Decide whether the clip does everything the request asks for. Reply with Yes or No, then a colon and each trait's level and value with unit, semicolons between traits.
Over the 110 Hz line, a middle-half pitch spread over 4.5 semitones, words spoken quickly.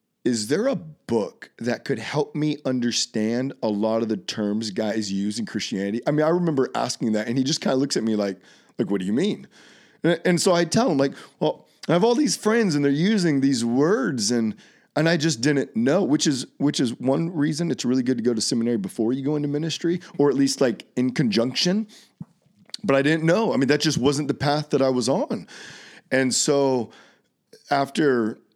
Yes: medium, 140 Hz; average, 5.1 semitones; fast, 220 wpm